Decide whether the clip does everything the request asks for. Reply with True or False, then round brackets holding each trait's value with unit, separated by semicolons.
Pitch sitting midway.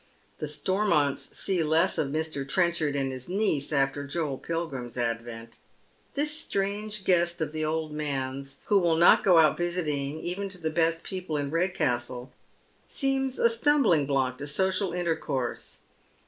True (160 Hz)